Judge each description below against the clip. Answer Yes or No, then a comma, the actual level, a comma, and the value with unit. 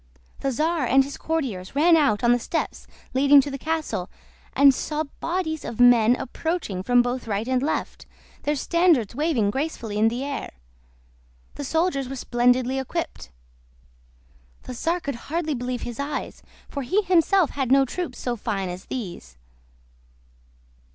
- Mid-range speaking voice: No, very high, 270 Hz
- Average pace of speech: Yes, average, 155 wpm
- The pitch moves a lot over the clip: No, average, 4.7 semitones